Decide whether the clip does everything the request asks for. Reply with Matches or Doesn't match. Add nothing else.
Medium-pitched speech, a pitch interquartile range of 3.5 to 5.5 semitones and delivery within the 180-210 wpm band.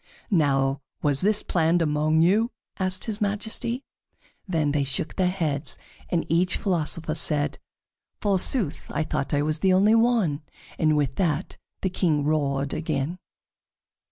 Doesn't match